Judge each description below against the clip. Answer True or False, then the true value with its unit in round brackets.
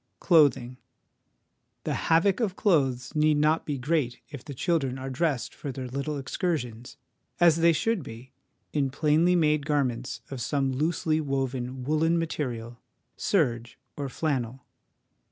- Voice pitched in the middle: True (145 Hz)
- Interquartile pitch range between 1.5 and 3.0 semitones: False (3.9 semitones)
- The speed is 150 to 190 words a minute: False (135 wpm)